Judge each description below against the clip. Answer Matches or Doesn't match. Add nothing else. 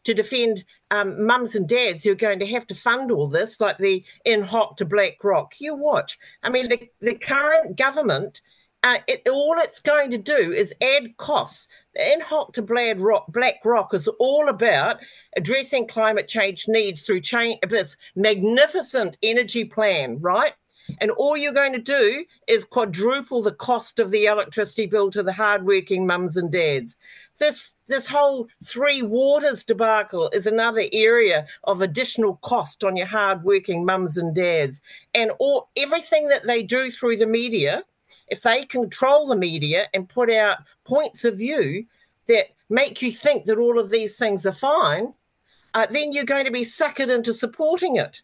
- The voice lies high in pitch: Matches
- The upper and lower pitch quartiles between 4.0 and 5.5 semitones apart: Matches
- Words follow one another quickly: Doesn't match